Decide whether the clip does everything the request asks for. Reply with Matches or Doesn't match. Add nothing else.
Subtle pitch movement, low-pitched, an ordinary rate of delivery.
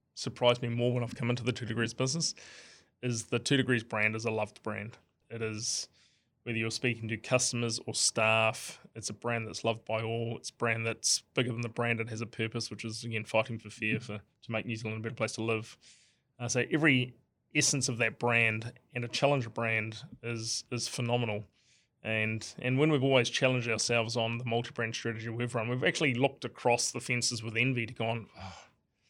Doesn't match